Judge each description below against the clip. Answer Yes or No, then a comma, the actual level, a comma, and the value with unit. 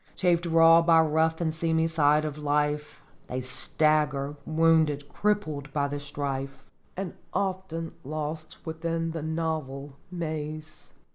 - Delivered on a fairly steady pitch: Yes, narrow, 1.9 semitones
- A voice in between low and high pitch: Yes, medium, 155 Hz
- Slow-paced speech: Yes, slow, 125 wpm